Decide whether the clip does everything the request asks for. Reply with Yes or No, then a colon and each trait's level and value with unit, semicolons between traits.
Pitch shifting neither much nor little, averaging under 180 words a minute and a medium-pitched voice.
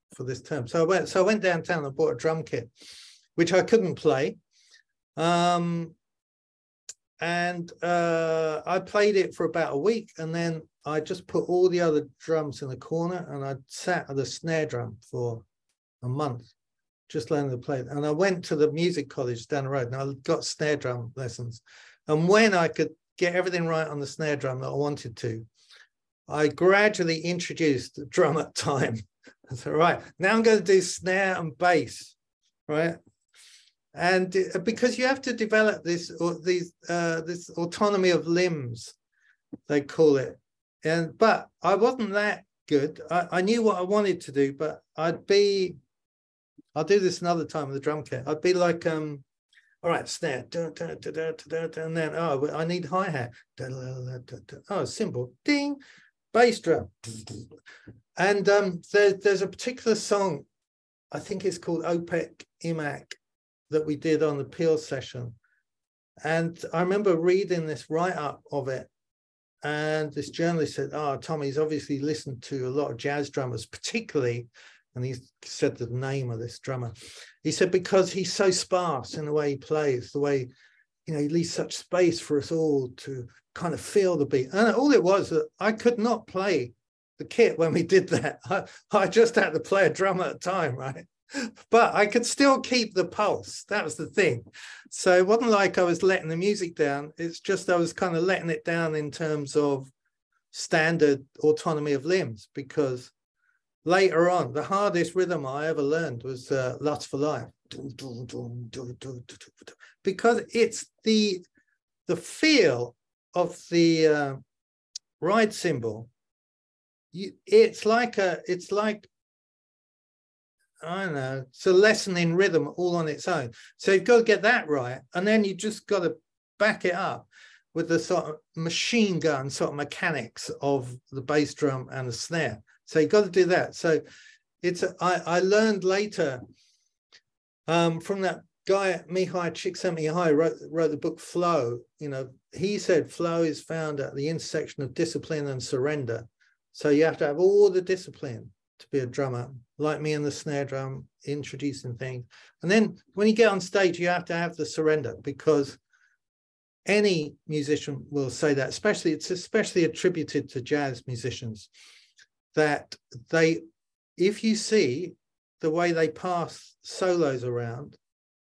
Yes: average, 4.7 semitones; average, 170 wpm; medium, 160 Hz